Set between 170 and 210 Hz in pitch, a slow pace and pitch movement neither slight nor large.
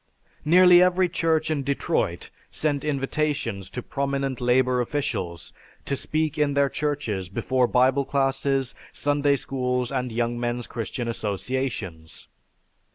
No: low, 135 Hz; slow, 120 wpm; average, 3.1 semitones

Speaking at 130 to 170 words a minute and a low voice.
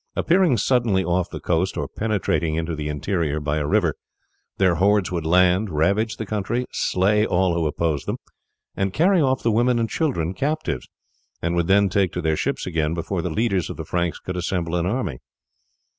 No: average, 190 wpm; very low, 90 Hz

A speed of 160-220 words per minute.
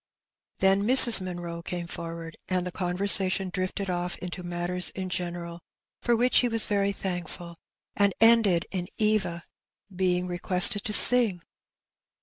No: slow, 135 wpm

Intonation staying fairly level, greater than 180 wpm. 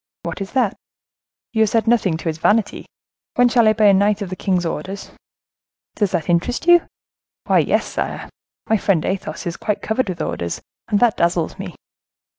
No: average, 4.0 semitones; average, 190 wpm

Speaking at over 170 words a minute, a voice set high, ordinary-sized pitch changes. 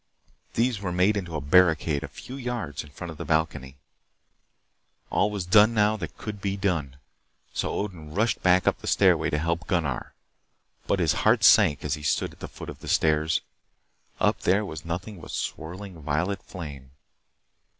No: average, 180 wpm; very low, 90 Hz; average, 4.7 semitones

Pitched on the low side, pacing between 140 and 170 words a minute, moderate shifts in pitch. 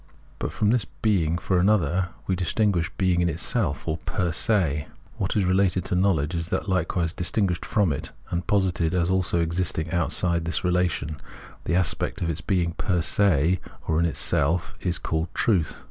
No: very low, 90 Hz; average, 165 wpm; narrow, 2.3 semitones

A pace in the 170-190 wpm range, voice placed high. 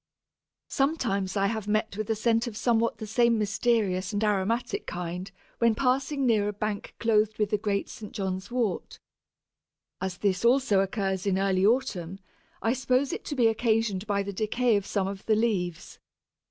Yes: average, 175 wpm; high, 215 Hz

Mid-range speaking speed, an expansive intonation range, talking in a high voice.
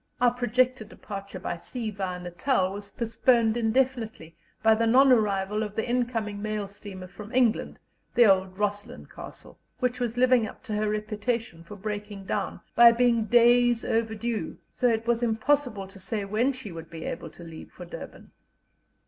No: average, 175 wpm; average, 3.2 semitones; high, 220 Hz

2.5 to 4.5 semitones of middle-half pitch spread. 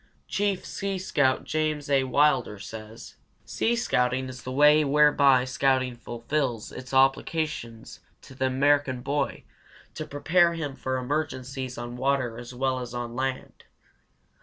Yes: average, 2.9 semitones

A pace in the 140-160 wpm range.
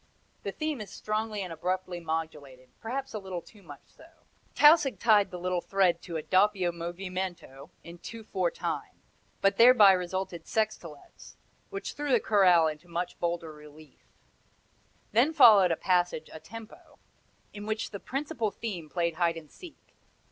Yes: average, 155 wpm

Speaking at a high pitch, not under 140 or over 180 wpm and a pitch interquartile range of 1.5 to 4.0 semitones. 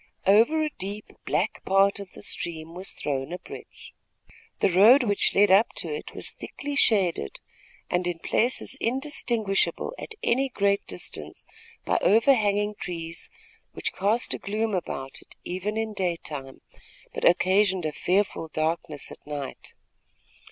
No: high, 195 Hz; average, 145 wpm; average, 4.4 semitones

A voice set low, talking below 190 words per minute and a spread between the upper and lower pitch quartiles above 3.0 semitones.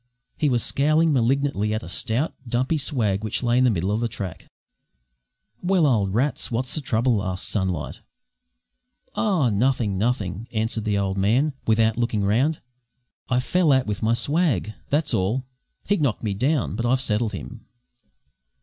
Yes: low, 120 Hz; average, 165 wpm; average, 4.6 semitones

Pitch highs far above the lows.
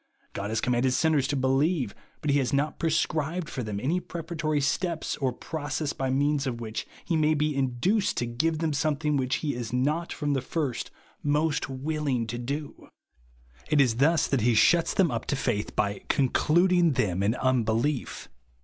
No: average, 4.0 semitones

